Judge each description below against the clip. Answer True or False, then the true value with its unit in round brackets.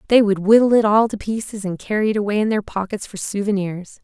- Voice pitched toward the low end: False (205 Hz)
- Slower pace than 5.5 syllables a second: False (6.0 syllables/s)